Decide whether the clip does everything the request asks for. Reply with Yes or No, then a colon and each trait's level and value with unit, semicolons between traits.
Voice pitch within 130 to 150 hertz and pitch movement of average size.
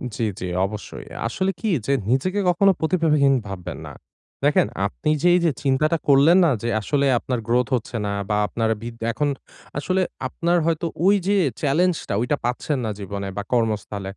No: medium, 140 Hz; wide, 6.7 semitones